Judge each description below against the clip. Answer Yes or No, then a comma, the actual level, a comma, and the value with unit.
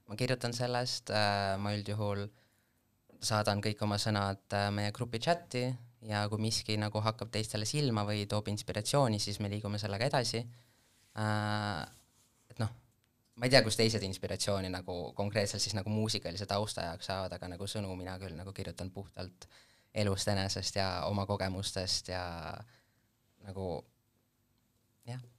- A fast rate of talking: No, average, 145 wpm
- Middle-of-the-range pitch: No, low, 105 Hz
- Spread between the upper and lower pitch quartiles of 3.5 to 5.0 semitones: No, average, 2.7 semitones